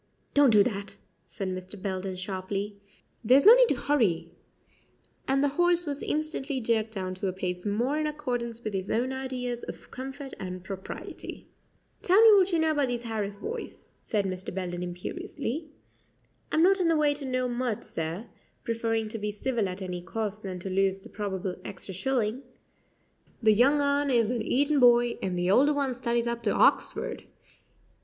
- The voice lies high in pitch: Yes, high, 235 Hz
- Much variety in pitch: Yes, wide, 6.3 semitones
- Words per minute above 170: Yes, average, 180 wpm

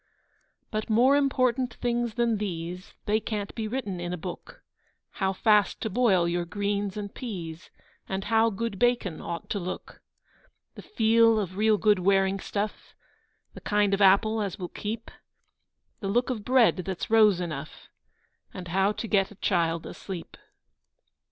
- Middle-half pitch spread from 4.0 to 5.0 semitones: No, average, 3.3 semitones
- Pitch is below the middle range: No, high, 205 Hz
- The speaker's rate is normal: Yes, average, 160 wpm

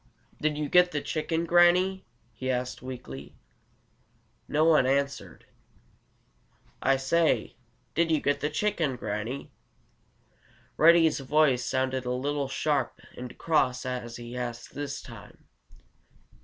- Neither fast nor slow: No, slow, 120 wpm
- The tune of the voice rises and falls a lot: No, average, 3.9 semitones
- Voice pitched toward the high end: No, medium, 140 Hz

